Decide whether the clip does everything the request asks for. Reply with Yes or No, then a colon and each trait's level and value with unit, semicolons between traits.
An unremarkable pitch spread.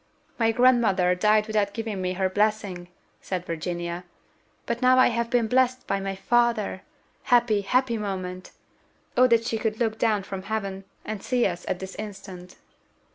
Yes: average, 3.6 semitones